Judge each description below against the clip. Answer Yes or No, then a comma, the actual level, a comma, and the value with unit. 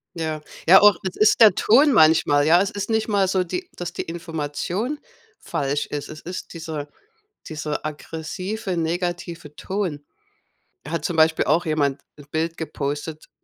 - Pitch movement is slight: No, average, 3.7 semitones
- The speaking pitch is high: No, medium, 165 Hz